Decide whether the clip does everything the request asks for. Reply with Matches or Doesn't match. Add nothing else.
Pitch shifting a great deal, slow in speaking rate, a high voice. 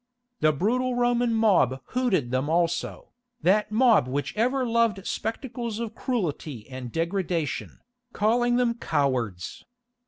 Matches